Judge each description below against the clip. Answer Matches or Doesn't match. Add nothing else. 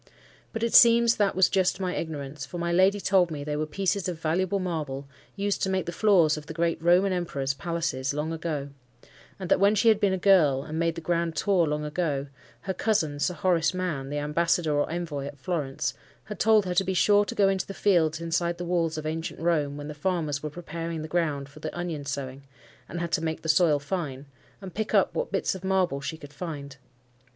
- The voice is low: Doesn't match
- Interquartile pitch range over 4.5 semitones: Doesn't match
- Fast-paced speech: Matches